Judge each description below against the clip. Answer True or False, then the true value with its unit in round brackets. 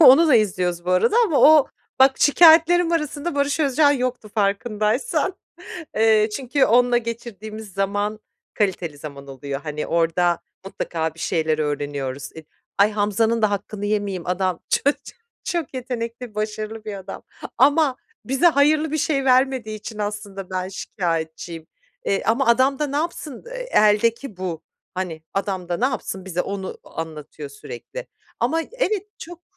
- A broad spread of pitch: True (6.9 semitones)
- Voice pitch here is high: True (215 Hz)